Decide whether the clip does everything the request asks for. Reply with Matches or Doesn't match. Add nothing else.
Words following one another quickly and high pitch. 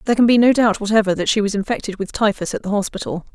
Matches